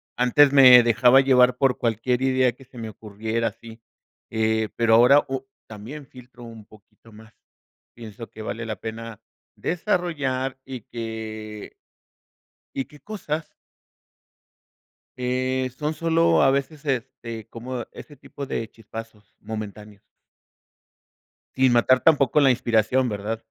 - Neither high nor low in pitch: No, low, 120 Hz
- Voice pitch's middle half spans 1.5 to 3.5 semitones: Yes, average, 3.1 semitones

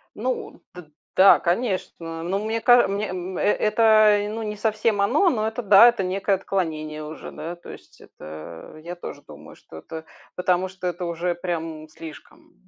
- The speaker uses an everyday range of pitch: Yes, average, 4.2 semitones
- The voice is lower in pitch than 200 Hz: Yes, medium, 185 Hz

